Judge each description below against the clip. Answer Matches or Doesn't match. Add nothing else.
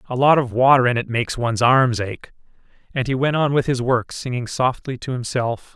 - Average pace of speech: Doesn't match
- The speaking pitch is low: Matches